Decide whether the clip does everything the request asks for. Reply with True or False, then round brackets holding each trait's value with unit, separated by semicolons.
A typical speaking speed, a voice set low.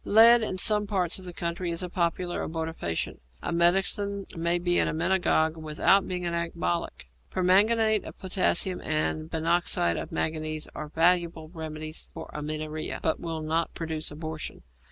False (155 wpm; 170 Hz)